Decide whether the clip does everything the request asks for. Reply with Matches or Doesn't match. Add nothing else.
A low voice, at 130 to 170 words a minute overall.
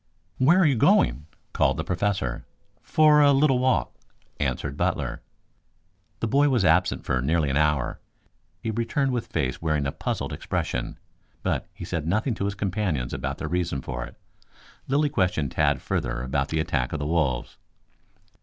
Matches